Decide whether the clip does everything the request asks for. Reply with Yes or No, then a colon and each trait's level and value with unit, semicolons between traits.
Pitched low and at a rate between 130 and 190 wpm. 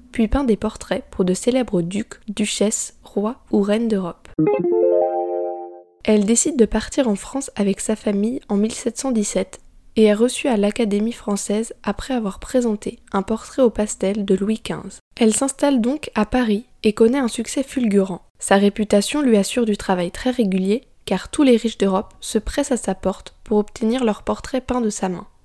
No: high, 215 Hz; average, 180 wpm